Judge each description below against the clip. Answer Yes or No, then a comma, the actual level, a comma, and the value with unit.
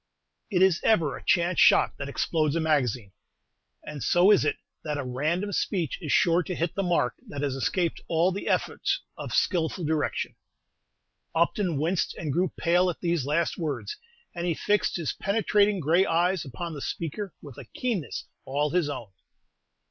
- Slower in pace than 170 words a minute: No, average, 175 wpm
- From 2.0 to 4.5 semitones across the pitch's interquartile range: Yes, average, 3.5 semitones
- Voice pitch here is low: No, medium, 170 Hz